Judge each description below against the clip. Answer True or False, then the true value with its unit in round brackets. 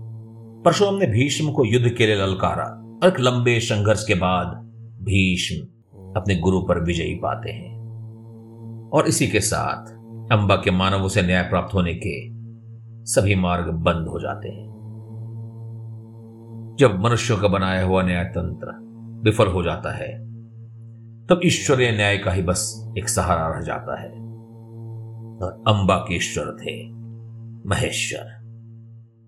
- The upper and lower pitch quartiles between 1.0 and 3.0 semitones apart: True (2.7 semitones)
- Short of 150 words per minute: True (135 wpm)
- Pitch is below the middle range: True (115 Hz)